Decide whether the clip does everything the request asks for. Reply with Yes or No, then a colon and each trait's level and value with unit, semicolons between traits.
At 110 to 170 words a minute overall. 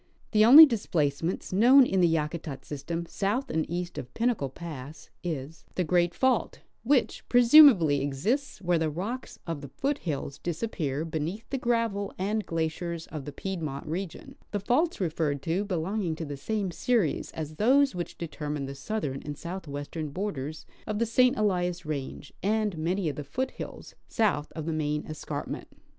Yes: average, 165 wpm